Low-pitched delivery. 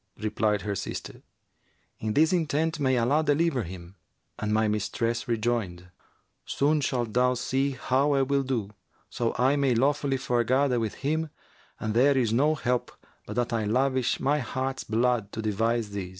Yes: low, 125 Hz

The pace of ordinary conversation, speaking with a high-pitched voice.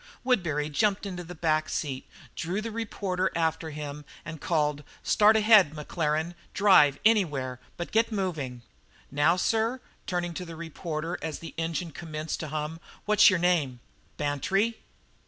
No: average, 145 wpm; medium, 165 Hz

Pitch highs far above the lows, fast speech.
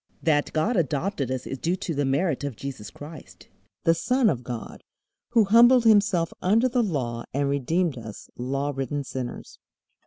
No: wide, 6.4 semitones; average, 165 wpm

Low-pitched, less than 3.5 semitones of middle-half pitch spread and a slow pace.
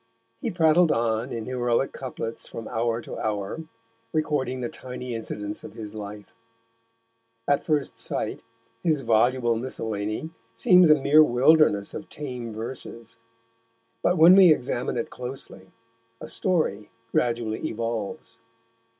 No: low, 120 Hz; average, 4.9 semitones; slow, 125 wpm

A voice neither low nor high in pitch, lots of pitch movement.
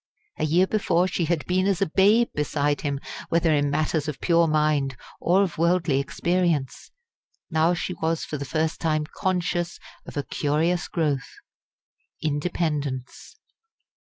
No: medium, 160 Hz; average, 3.1 semitones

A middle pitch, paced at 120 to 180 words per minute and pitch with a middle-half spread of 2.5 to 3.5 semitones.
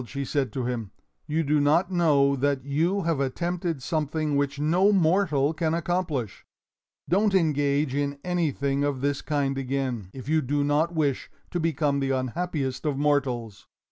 Yes: medium, 145 Hz; average, 160 wpm; average, 3.1 semitones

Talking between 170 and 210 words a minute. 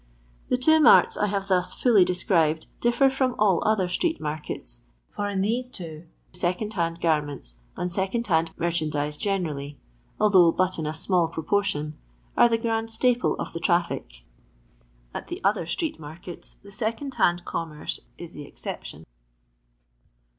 No: average, 155 wpm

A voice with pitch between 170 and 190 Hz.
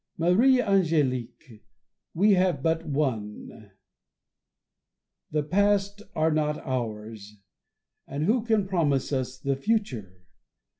No: medium, 150 Hz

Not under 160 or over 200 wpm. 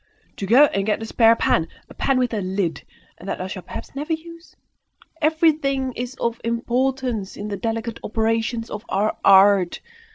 Yes: average, 175 wpm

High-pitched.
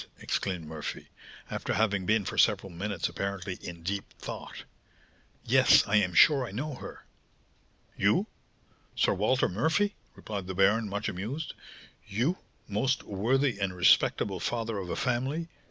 No: low, 105 Hz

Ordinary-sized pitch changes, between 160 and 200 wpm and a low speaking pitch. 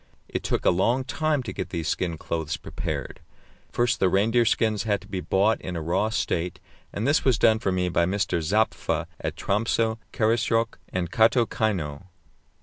Yes: average, 4.0 semitones; average, 175 wpm; low, 105 Hz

